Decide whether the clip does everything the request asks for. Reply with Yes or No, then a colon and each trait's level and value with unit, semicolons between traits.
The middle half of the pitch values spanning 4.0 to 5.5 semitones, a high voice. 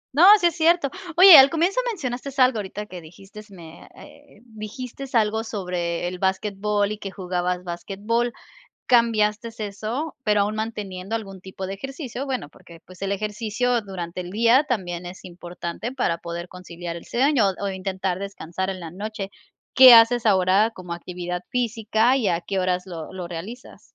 Yes: average, 4.5 semitones; high, 205 Hz